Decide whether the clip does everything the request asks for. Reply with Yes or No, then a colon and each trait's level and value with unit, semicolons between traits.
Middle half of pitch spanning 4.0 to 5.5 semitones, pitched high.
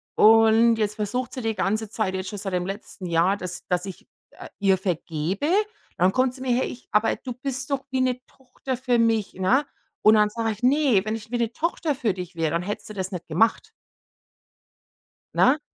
Yes: average, 4.8 semitones; high, 220 Hz